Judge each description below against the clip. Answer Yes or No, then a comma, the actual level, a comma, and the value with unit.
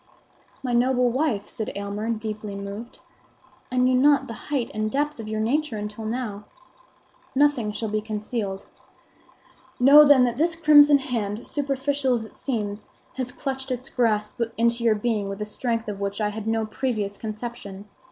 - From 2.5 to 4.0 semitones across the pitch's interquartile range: Yes, average, 3.7 semitones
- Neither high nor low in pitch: No, high, 230 Hz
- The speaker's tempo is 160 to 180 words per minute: Yes, average, 165 wpm